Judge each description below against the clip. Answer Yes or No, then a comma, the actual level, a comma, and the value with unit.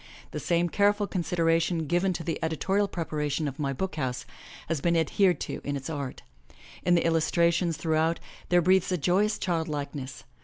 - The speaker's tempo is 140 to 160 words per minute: No, average, 175 wpm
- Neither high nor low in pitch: Yes, medium, 165 Hz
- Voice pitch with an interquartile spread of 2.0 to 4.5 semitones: Yes, average, 2.7 semitones